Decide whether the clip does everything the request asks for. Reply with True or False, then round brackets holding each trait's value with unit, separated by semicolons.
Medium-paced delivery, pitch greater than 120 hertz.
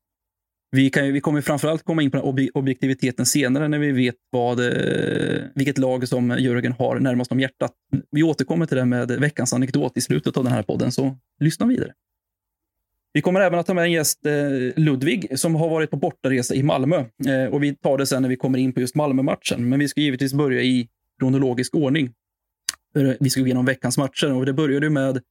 False (200 wpm; 135 Hz)